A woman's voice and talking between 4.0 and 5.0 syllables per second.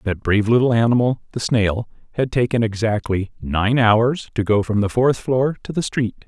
No: male; 4.8 syllables/s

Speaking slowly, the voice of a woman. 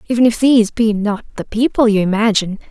No: average, 200 wpm; female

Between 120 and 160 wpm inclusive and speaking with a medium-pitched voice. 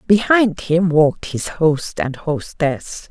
Yes: slow, 135 wpm; medium, 165 Hz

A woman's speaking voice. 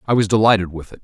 No: male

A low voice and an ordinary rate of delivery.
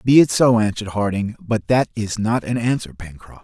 No: low, 110 Hz; fast, 210 wpm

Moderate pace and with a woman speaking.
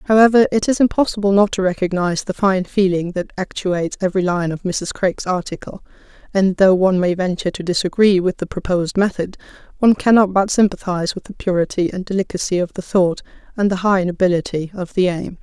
Yes: average, 185 wpm; female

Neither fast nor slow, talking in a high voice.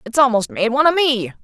No: fast, 250 wpm; high, 245 Hz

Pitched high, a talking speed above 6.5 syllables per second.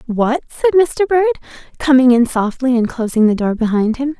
No: very high, 255 Hz; 5.5 syllables/s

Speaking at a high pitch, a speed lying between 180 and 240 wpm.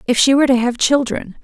No: very high, 255 Hz; fast, 250 wpm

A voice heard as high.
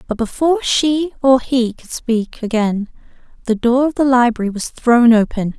Yes: high, 245 Hz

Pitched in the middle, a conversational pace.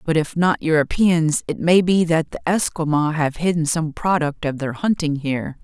Yes: medium, 160 Hz; average, 190 wpm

